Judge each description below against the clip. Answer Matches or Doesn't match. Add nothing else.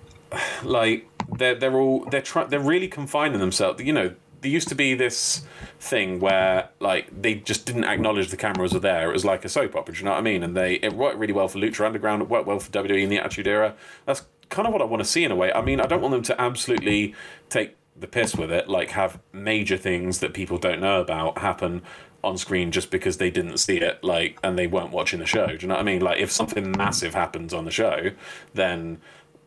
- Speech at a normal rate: Doesn't match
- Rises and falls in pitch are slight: Doesn't match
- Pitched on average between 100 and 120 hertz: Matches